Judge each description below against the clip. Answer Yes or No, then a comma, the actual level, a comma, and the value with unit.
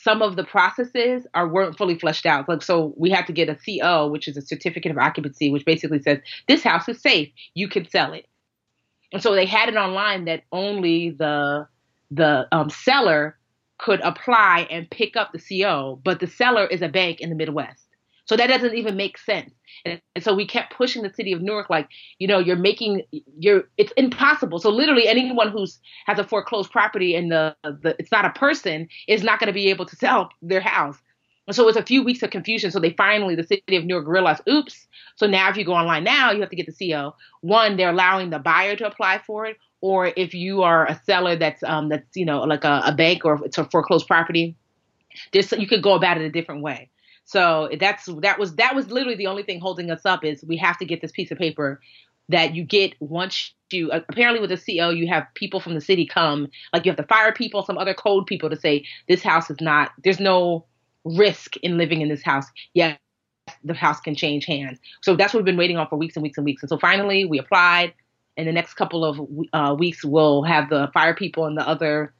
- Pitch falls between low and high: Yes, medium, 175 Hz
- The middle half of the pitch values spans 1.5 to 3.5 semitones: No, average, 4.3 semitones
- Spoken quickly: Yes, fast, 230 wpm